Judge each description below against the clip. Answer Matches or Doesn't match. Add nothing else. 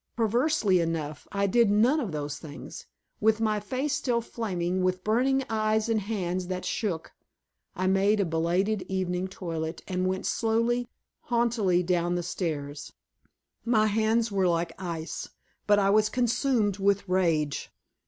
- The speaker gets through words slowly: Doesn't match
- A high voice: Matches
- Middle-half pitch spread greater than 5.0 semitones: Doesn't match